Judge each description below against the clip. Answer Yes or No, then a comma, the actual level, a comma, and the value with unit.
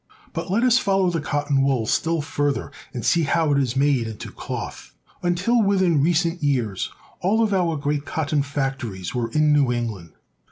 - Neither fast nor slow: Yes, average, 175 wpm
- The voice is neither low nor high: Yes, medium, 145 Hz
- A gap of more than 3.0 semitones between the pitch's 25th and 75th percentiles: Yes, average, 4.6 semitones